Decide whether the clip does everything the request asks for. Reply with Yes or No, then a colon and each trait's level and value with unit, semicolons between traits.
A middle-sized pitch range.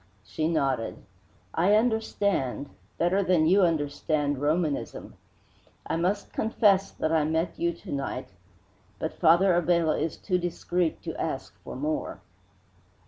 Yes: average, 3.3 semitones